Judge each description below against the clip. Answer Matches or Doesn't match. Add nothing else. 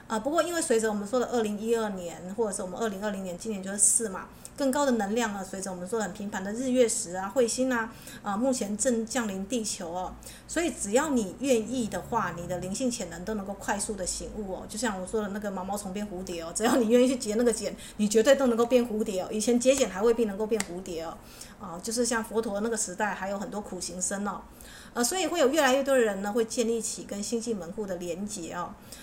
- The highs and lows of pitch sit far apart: Doesn't match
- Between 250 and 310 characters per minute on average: Doesn't match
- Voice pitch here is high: Matches